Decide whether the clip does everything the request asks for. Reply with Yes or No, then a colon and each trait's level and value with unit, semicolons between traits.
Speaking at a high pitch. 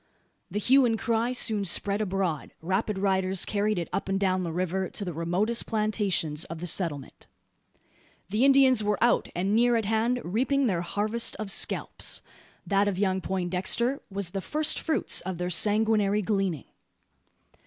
Yes: high, 200 Hz